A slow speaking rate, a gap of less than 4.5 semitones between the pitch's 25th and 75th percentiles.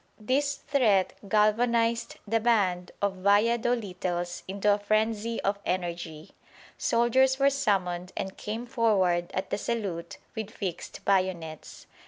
Yes: slow, 125 wpm; average, 4.0 semitones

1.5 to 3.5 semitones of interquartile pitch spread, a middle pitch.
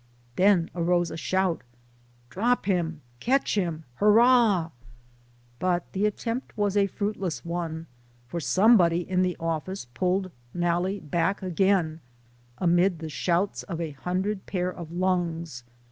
Yes: average, 3.0 semitones; medium, 175 Hz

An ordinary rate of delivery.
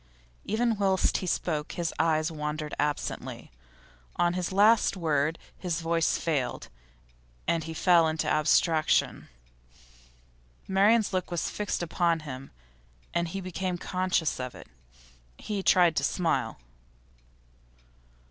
No: slow, 120 wpm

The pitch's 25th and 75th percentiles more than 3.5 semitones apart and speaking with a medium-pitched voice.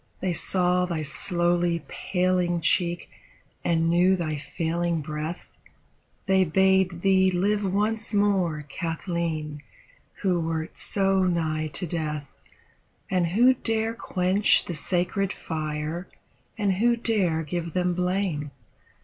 No: average, 2.7 semitones; medium, 175 Hz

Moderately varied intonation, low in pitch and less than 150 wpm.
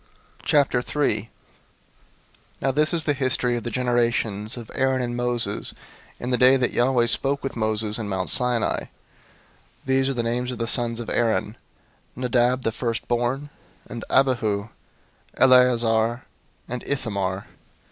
No: narrow, 2.1 semitones; low, 120 Hz; average, 140 wpm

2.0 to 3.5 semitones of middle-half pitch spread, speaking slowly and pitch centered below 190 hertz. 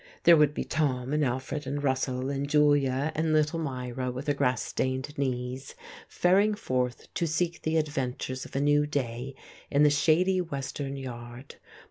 No: average, 2.8 semitones; average, 165 wpm; medium, 140 Hz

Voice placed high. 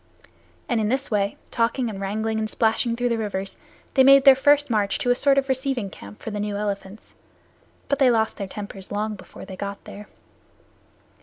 Yes: high, 220 Hz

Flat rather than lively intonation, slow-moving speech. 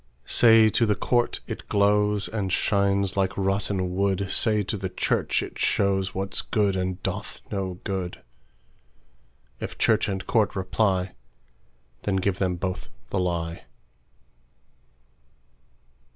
Yes: narrow, 1.8 semitones; slow, 110 wpm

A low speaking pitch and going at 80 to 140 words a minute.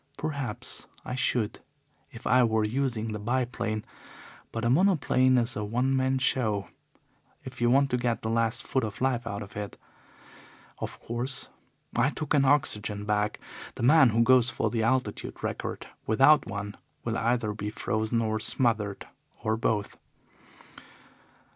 No: low, 115 Hz; average, 155 wpm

